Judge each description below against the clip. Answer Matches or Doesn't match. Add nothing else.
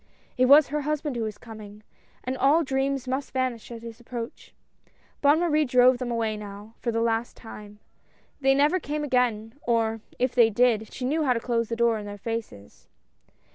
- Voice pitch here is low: Doesn't match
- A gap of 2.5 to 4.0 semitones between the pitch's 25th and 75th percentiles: Matches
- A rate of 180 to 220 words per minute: Matches